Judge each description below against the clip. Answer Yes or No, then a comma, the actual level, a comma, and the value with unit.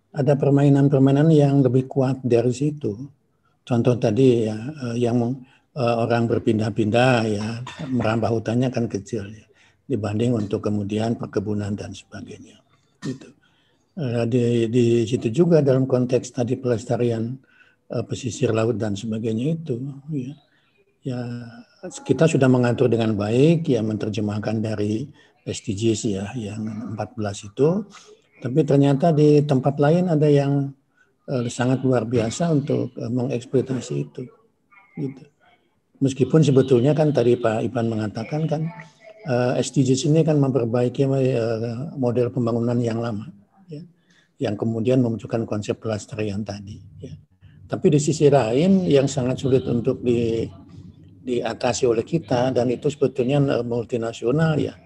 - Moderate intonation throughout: Yes, average, 3.6 semitones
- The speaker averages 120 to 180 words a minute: Yes, average, 125 wpm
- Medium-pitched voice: No, low, 125 Hz